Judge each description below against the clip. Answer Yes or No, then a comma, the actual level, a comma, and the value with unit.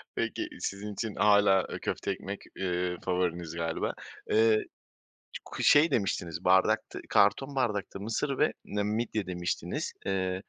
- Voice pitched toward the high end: No, low, 100 Hz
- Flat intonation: No, average, 3.2 semitones